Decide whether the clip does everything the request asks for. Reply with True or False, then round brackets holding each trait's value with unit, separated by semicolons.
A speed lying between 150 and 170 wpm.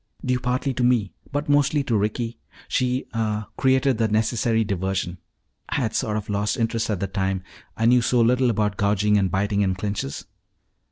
False (180 wpm)